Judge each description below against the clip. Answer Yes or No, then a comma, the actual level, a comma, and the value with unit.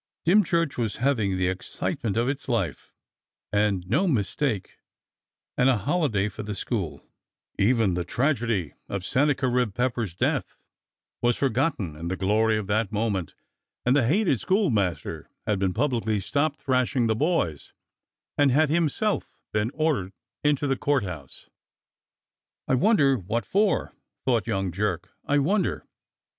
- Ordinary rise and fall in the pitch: No, wide, 6.3 semitones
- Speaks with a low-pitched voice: Yes, low, 115 Hz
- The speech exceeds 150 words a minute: No, average, 140 wpm